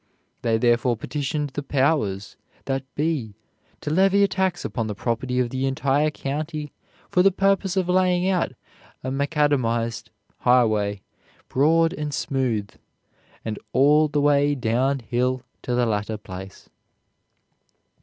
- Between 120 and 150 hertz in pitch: Yes, low, 135 Hz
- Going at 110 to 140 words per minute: Yes, slow, 135 wpm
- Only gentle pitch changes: No, average, 4.5 semitones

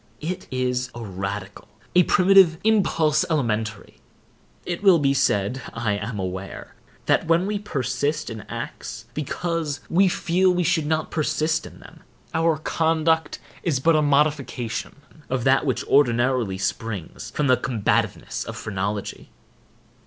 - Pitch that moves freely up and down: Yes, wide, 6.2 semitones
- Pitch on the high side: No, medium, 145 Hz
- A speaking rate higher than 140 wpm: No, slow, 135 wpm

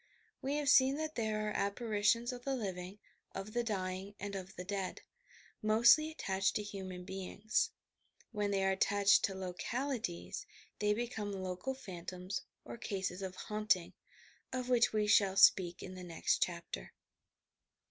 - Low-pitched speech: No, high, 205 Hz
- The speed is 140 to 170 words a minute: Yes, average, 160 wpm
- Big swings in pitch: No, average, 3.7 semitones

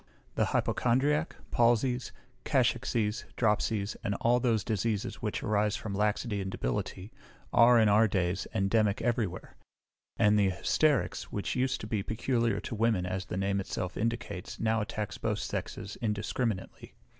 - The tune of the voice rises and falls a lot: No, average, 2.8 semitones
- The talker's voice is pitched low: Yes, low, 105 Hz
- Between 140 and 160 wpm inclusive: Yes, average, 150 wpm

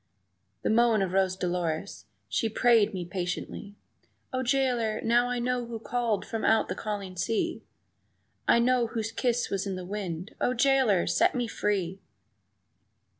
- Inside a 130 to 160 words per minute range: Yes, average, 155 wpm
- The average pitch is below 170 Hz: No, high, 220 Hz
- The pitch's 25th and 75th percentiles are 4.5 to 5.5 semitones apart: No, average, 4.0 semitones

